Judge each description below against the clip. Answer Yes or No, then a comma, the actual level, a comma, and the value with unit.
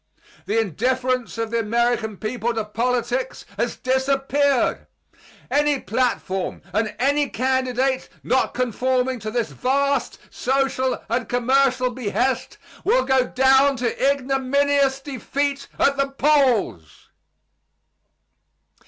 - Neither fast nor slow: No, slow, 105 wpm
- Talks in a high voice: Yes, very high, 255 Hz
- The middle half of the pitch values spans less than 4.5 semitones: Yes, narrow, 2.5 semitones